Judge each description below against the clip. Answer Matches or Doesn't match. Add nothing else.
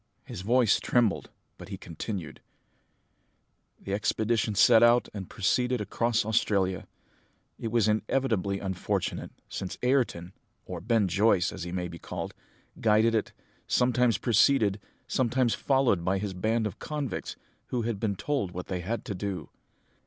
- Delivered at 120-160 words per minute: Matches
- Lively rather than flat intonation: Doesn't match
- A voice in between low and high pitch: Doesn't match